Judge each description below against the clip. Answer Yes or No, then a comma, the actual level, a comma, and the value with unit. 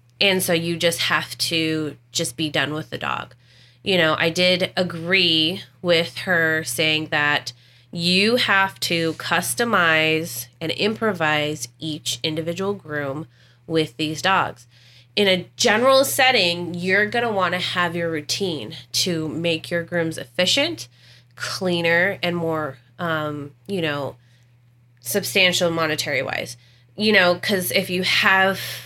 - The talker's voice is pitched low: No, medium, 165 Hz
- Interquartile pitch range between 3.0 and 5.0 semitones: Yes, average, 4.0 semitones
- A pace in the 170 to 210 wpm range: No, slow, 135 wpm